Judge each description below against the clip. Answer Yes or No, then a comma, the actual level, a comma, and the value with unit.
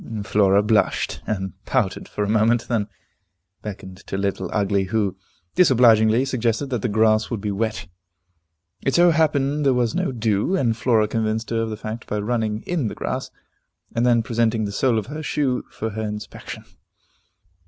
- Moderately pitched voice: No, low, 110 Hz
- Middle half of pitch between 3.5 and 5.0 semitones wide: No, average, 2.7 semitones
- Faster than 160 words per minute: Yes, average, 175 wpm